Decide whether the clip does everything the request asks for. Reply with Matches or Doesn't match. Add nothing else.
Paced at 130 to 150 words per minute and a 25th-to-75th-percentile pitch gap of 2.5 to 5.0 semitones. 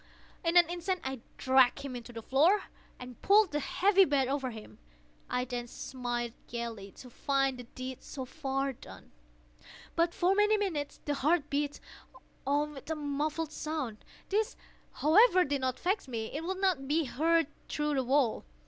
Doesn't match